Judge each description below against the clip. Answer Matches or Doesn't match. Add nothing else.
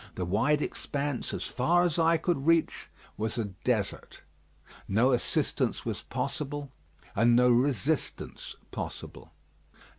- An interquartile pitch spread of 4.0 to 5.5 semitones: Matches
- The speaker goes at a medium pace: Doesn't match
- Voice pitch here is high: Doesn't match